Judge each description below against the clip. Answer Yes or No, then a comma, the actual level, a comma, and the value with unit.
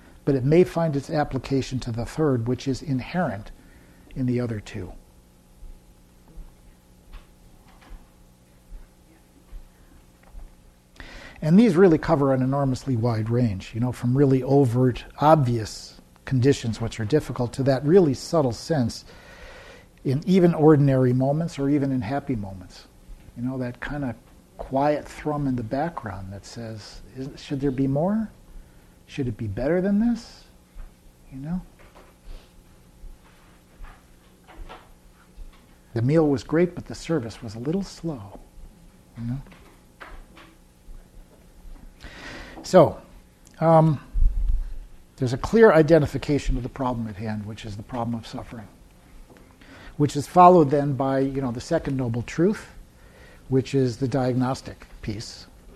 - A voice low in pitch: Yes, low, 120 Hz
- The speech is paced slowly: Yes, slow, 125 wpm